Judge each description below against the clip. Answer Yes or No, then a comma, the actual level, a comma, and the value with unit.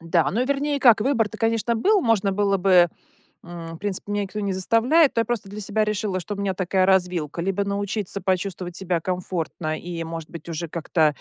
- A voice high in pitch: Yes, high, 195 Hz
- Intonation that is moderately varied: Yes, average, 3.5 semitones